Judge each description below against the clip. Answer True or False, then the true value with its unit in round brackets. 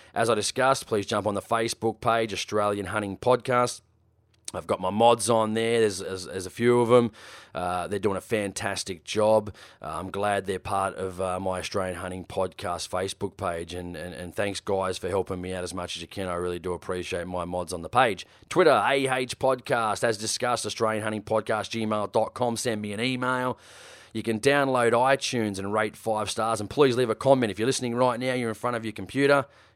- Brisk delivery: True (210 wpm)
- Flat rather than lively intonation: False (3.8 semitones)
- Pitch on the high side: False (110 Hz)